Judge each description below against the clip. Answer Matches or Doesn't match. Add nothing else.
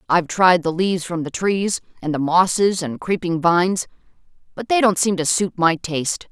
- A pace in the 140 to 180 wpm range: Doesn't match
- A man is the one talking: Doesn't match